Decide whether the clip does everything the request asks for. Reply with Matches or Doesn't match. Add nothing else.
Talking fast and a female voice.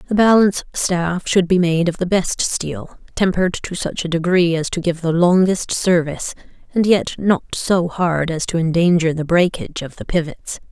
Doesn't match